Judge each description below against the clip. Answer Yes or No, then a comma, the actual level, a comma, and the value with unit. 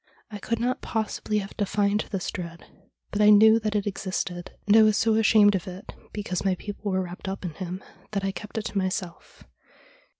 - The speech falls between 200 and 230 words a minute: Yes, fast, 205 wpm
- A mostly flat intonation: Yes, narrow, 2.2 semitones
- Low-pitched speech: No, high, 205 Hz